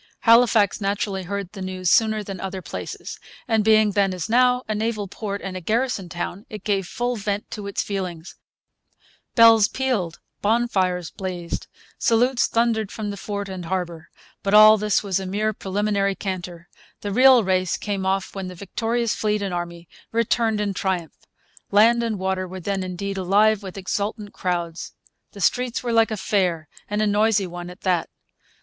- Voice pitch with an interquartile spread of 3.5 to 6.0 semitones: No, average, 2.7 semitones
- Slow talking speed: No, average, 175 wpm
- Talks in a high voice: Yes, high, 200 Hz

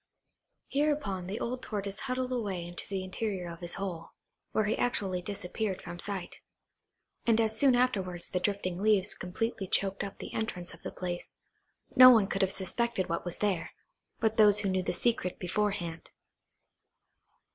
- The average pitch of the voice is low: No, high, 195 Hz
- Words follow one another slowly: No, average, 165 wpm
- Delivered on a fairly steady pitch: No, average, 3.4 semitones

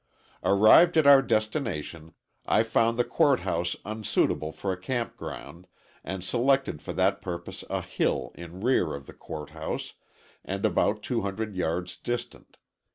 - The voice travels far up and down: Yes, wide, 5.9 semitones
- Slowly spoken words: No, average, 150 wpm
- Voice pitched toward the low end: Yes, low, 100 Hz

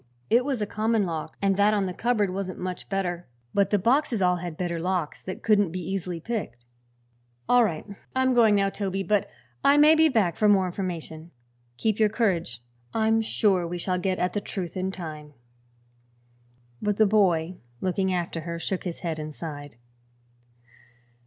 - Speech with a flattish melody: No, average, 3.5 semitones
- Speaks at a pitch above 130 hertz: Yes, high, 190 Hz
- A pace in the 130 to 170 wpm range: No, average, 180 wpm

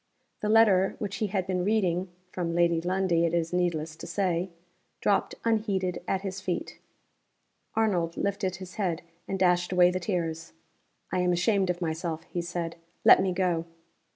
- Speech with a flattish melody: Yes, narrow, 2.0 semitones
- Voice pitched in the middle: Yes, medium, 180 Hz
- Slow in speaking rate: No, average, 165 wpm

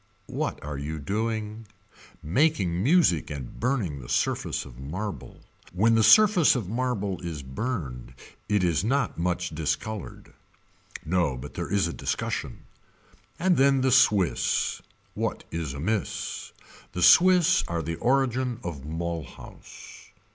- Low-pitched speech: Yes, very low, 95 Hz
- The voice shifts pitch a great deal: Yes, wide, 7.7 semitones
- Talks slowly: Yes, slow, 130 wpm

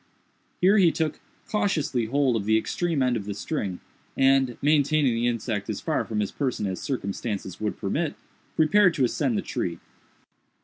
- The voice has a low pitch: Yes, low, 130 Hz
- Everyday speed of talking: Yes, average, 170 wpm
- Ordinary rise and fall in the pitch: No, wide, 6.2 semitones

